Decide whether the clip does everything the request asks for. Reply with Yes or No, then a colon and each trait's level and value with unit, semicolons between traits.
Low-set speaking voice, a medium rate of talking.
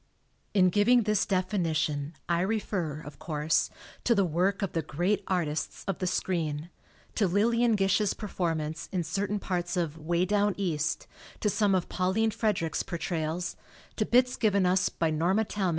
No: medium, 185 Hz; average, 165 wpm